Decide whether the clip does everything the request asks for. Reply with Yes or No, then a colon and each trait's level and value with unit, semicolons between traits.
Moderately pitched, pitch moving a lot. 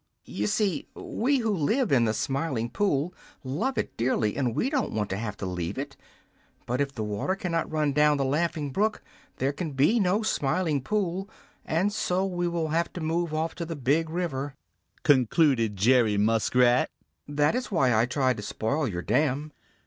Yes: medium, 145 Hz; wide, 5.8 semitones